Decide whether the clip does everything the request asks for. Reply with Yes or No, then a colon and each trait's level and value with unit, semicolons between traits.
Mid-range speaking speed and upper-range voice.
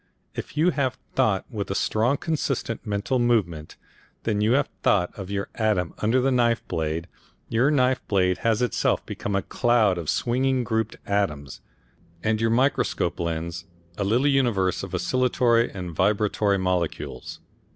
No: average, 155 wpm; low, 110 Hz